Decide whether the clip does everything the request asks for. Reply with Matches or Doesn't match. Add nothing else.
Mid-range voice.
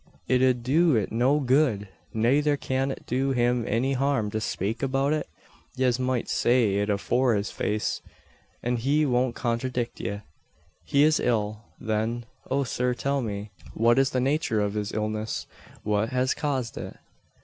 Doesn't match